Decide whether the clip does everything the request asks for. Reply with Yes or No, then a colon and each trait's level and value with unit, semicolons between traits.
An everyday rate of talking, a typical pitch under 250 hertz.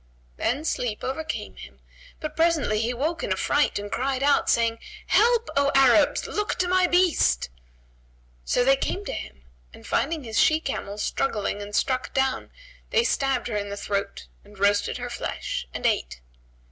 No: average, 170 wpm; very high, 265 Hz